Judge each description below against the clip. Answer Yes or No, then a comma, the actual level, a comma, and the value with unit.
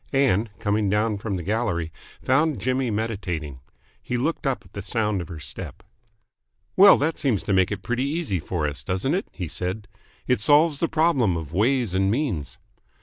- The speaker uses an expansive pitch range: Yes, wide, 6.4 semitones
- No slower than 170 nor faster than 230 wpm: Yes, average, 185 wpm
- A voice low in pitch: Yes, low, 105 Hz